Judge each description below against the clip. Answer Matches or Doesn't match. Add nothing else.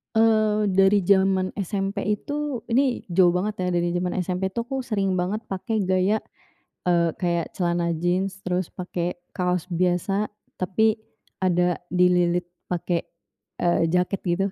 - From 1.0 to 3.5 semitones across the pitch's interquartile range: Matches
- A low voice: Doesn't match